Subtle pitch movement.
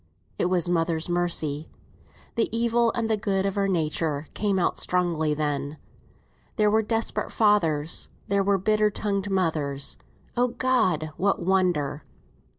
No: average, 4.8 semitones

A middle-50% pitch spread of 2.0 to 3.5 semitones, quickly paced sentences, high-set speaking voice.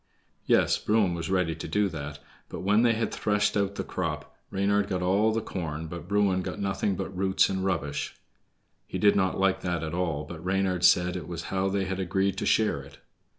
No: narrow, 2.5 semitones; fast, 210 wpm; very low, 95 Hz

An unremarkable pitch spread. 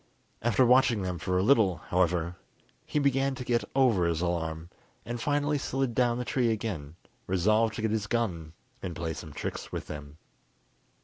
No: wide, 6.3 semitones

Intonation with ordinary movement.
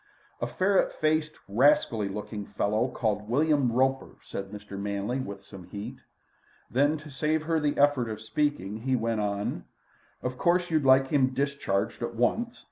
No: wide, 5.8 semitones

